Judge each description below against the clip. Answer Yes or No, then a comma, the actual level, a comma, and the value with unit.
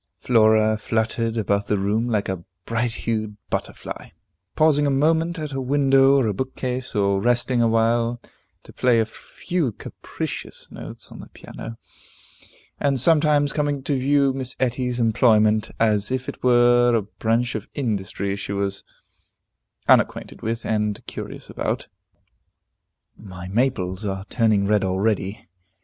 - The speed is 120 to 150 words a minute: Yes, average, 140 wpm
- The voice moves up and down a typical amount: Yes, average, 3.7 semitones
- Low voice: Yes, low, 115 Hz